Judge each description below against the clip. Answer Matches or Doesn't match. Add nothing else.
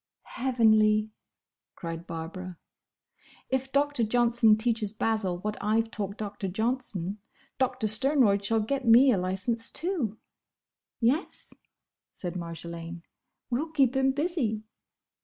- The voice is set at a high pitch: Matches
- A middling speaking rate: Doesn't match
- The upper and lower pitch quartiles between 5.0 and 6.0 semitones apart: Doesn't match